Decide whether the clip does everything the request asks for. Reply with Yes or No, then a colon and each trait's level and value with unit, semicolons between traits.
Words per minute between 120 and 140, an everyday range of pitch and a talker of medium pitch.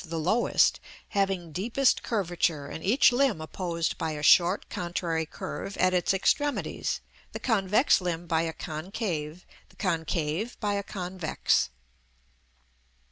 Yes: slow, 135 wpm; average, 3.8 semitones; medium, 180 Hz